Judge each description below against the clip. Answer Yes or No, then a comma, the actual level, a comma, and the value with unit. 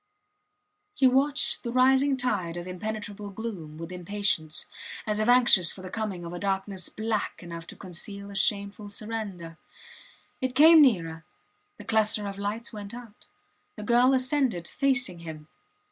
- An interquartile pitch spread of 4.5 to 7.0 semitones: Yes, average, 4.8 semitones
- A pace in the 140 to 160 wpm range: Yes, average, 150 wpm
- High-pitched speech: Yes, high, 205 Hz